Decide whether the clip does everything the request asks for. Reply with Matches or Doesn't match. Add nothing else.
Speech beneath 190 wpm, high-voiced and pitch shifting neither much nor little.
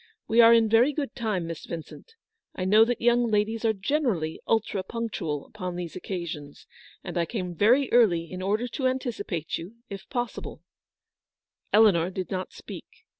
Matches